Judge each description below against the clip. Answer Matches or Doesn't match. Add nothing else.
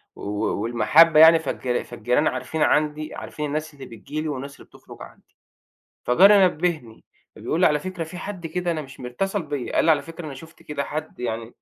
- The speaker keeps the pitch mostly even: Doesn't match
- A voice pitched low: Doesn't match